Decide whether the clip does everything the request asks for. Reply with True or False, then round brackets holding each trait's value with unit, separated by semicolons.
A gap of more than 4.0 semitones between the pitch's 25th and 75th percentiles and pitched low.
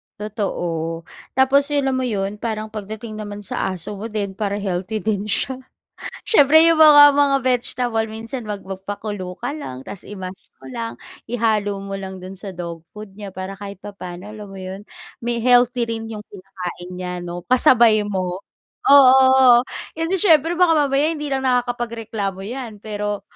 False (4.5 semitones; 215 Hz)